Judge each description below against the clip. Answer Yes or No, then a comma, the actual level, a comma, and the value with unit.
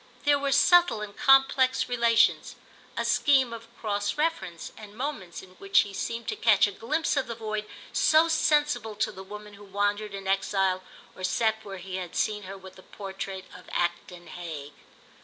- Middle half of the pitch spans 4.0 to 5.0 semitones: Yes, average, 4.6 semitones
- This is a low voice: No, high, 210 Hz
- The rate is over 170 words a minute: Yes, average, 180 wpm